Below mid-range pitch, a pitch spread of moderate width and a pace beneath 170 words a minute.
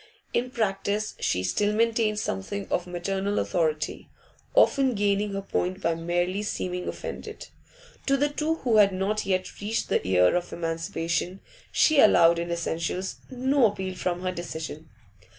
No: high, 190 Hz; average, 3.7 semitones; average, 150 wpm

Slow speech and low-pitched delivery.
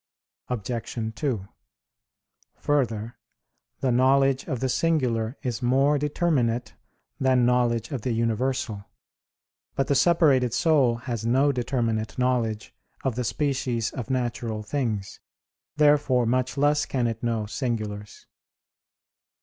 Yes: slow, 115 wpm; low, 125 Hz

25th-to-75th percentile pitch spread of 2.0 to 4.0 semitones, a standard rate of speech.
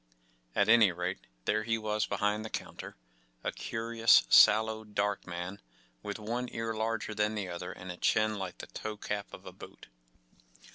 Yes: average, 3.1 semitones; average, 170 wpm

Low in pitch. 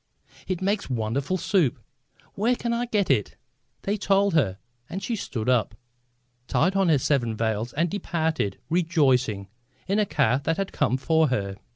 No: medium, 160 Hz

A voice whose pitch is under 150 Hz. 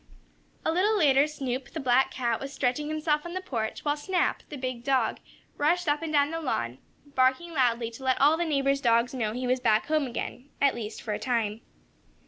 No: very high, 270 Hz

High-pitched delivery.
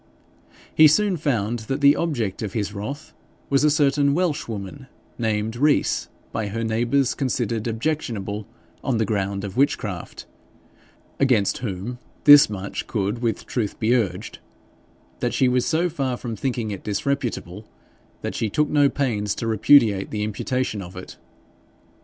No: low, 115 Hz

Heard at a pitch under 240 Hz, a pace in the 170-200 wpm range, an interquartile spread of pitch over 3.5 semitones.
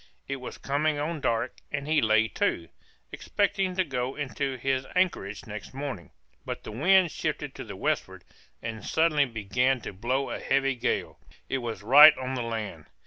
Yes: low, 135 Hz; average, 175 wpm; average, 4.4 semitones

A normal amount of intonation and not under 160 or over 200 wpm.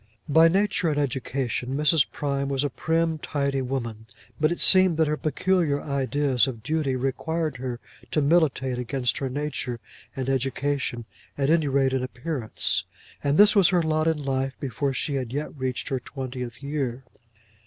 Yes: average, 3.0 semitones; average, 165 wpm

